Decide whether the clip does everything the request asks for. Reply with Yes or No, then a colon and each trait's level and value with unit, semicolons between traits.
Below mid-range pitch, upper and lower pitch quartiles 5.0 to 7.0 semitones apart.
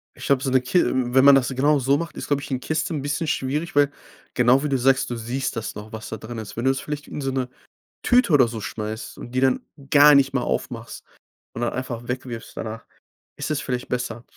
No: low, 130 Hz; average, 2.8 semitones